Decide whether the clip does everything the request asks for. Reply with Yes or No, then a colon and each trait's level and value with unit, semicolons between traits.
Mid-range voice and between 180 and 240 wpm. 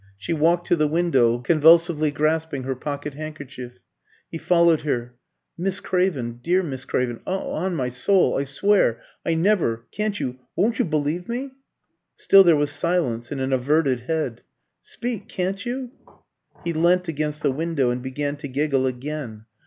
No: medium, 155 Hz; average, 160 wpm